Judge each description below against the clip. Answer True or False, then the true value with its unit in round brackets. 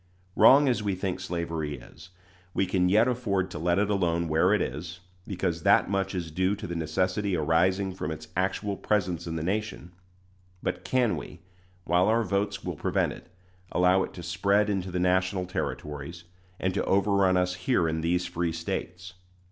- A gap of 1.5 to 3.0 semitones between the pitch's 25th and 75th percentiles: True (2.5 semitones)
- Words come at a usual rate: True (180 wpm)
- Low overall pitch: True (90 Hz)